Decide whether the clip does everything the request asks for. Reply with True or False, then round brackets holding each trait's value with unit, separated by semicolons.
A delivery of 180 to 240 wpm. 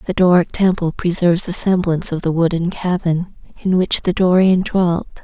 False (170 wpm)